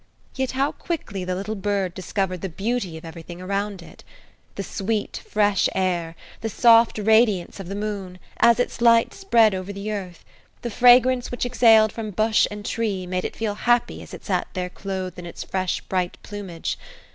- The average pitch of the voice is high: Yes, high, 205 Hz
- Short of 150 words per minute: No, average, 180 wpm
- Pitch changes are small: No, average, 3.5 semitones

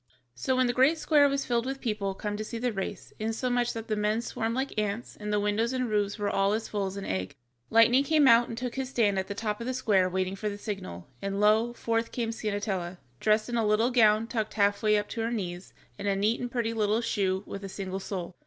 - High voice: Yes, high, 215 Hz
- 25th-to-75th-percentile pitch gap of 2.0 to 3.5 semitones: Yes, average, 2.8 semitones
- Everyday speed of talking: No, fast, 255 wpm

